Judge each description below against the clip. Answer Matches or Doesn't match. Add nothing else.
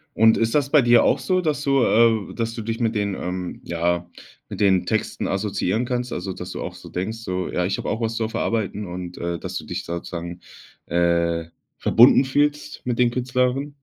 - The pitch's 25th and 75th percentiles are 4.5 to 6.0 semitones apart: Matches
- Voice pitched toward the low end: Matches